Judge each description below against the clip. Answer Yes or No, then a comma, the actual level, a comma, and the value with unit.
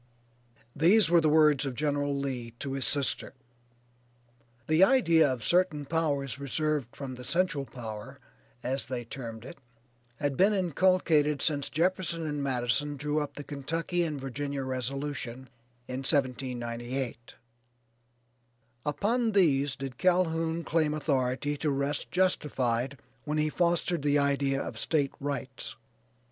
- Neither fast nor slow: No, slow, 130 wpm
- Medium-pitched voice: Yes, medium, 145 Hz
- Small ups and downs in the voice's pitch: No, average, 3.4 semitones